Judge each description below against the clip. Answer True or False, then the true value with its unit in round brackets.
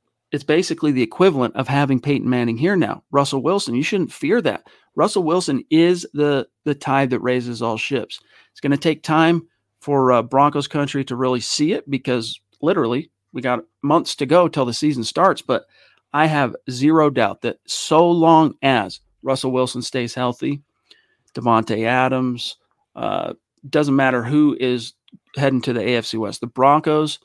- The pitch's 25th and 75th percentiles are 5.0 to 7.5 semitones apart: False (3.3 semitones)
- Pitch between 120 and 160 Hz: True (135 Hz)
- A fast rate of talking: False (170 wpm)